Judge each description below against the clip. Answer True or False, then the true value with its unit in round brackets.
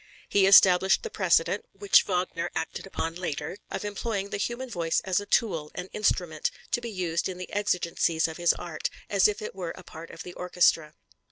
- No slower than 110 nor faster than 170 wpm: False (195 wpm)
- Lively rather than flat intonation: False (3.4 semitones)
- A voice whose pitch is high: False (180 Hz)